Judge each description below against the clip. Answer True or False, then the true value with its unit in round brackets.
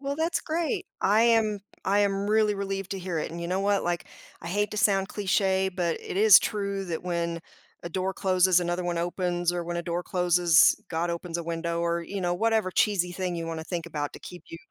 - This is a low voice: False (180 Hz)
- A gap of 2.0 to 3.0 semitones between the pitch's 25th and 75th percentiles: True (2.7 semitones)